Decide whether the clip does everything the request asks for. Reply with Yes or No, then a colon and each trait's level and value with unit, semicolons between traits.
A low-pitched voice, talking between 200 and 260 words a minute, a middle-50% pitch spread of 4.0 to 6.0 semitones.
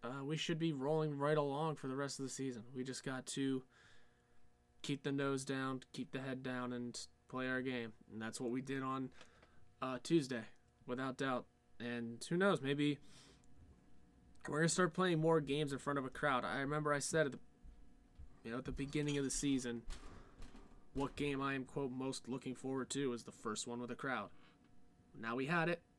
No: low, 130 Hz; fast, 205 wpm; average, 2.7 semitones